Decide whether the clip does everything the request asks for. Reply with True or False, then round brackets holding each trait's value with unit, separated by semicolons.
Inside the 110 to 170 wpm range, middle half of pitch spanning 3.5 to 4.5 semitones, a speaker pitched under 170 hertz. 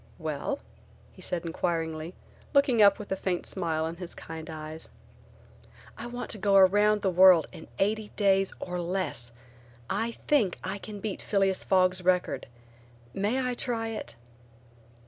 False (145 wpm; 3.8 semitones; 190 Hz)